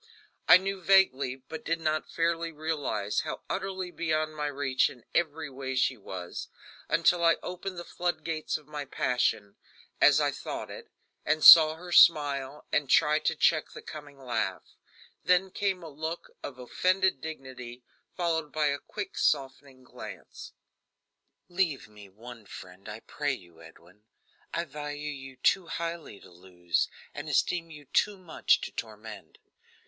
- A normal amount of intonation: Yes, average, 4.6 semitones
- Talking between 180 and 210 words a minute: No, average, 155 wpm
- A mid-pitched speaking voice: Yes, medium, 150 Hz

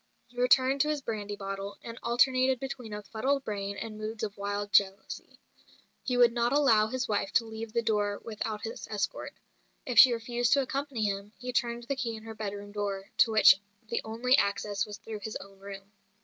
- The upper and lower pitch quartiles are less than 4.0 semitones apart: Yes, average, 3.1 semitones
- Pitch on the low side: No, high, 220 Hz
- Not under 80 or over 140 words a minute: No, average, 200 wpm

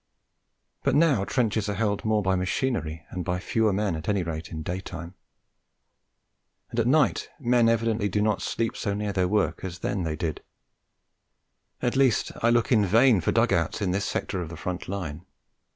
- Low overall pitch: Yes, low, 100 Hz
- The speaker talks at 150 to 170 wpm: No, average, 185 wpm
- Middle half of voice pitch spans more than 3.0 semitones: Yes, average, 4.1 semitones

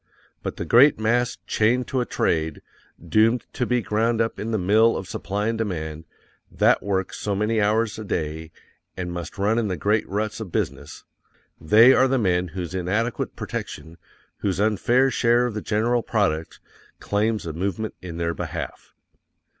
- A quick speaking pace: No, average, 170 wpm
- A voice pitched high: No, low, 105 Hz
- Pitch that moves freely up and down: No, average, 4.1 semitones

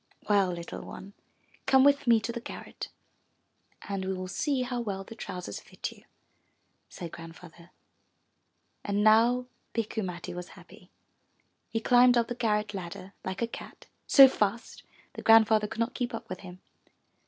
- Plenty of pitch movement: No, average, 4.1 semitones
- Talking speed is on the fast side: No, average, 165 wpm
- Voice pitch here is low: No, high, 210 Hz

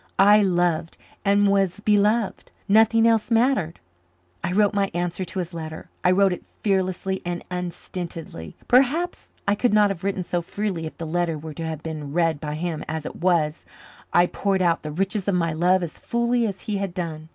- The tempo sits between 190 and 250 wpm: Yes, average, 195 wpm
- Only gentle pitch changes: No, average, 3.5 semitones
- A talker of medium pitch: Yes, medium, 180 Hz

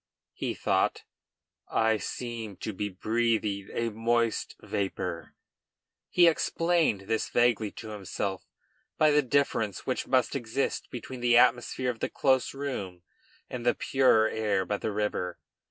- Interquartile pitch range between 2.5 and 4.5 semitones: Yes, average, 3.5 semitones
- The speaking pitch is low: Yes, low, 115 Hz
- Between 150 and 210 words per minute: No, average, 140 wpm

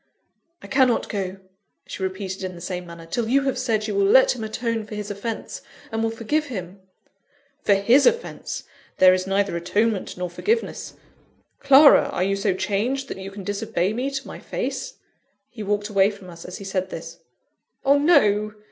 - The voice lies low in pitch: No, high, 205 Hz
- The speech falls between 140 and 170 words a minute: No, average, 185 wpm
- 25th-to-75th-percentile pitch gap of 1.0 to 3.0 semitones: No, average, 4.2 semitones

